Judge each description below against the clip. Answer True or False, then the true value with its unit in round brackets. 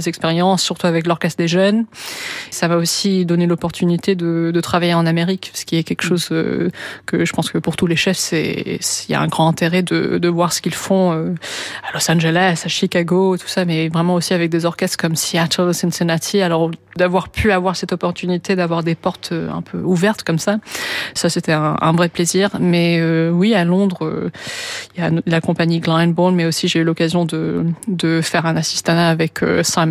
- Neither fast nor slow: True (210 wpm)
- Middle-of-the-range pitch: True (170 Hz)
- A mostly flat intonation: True (1.7 semitones)